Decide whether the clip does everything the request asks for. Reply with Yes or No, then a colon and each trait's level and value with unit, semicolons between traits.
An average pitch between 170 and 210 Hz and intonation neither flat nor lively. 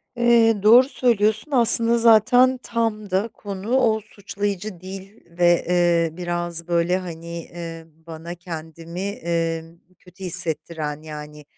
Yes: medium, 185 Hz; average, 4.7 semitones